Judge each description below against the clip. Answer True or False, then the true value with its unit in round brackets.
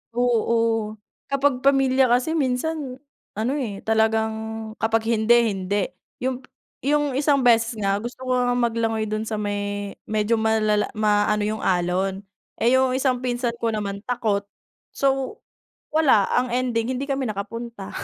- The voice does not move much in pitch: False (3.2 semitones)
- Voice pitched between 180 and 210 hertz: False (230 Hz)